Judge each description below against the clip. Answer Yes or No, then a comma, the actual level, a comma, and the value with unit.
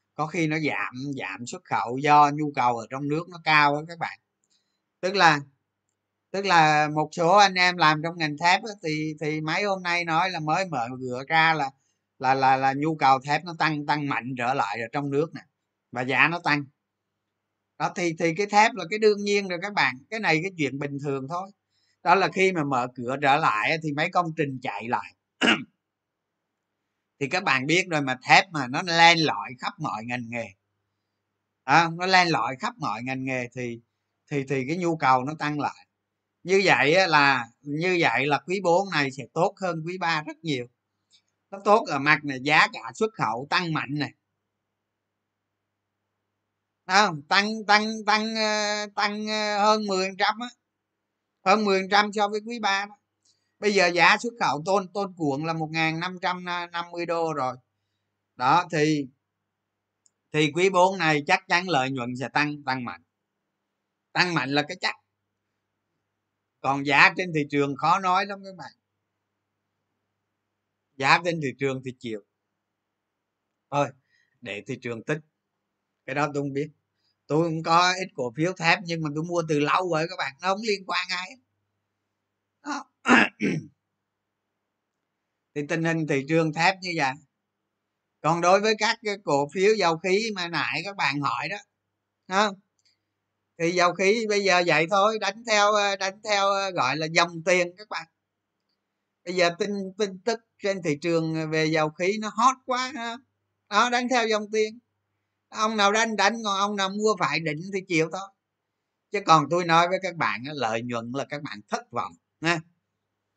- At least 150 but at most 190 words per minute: Yes, average, 180 wpm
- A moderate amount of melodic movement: No, wide, 8.7 semitones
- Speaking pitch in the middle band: Yes, medium, 150 Hz